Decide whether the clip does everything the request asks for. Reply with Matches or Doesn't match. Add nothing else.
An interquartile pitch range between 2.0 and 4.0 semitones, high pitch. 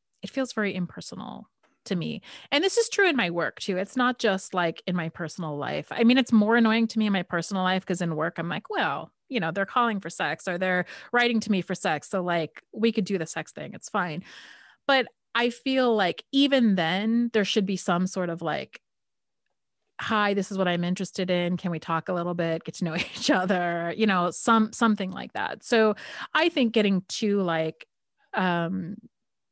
Doesn't match